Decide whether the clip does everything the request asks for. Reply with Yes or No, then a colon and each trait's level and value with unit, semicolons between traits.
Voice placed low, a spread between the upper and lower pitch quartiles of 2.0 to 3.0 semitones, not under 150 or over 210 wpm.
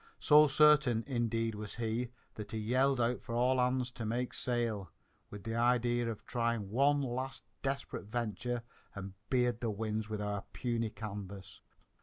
Yes: low, 120 Hz; narrow, 2.4 semitones; average, 160 wpm